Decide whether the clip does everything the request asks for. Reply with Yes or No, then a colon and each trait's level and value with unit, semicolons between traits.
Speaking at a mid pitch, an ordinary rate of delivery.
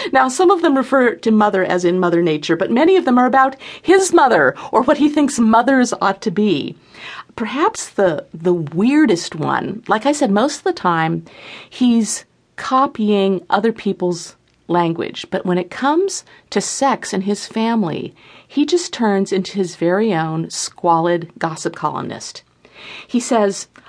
No: high, 210 Hz; average, 165 wpm